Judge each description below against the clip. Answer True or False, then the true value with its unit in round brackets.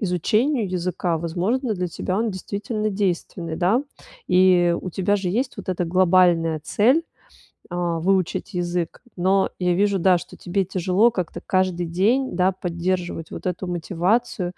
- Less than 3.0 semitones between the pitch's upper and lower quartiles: True (2.4 semitones)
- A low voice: False (185 Hz)